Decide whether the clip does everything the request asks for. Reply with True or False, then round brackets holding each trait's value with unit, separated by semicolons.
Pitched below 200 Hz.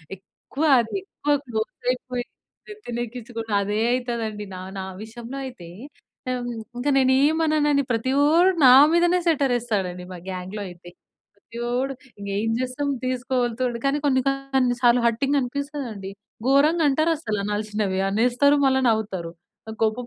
False (245 Hz)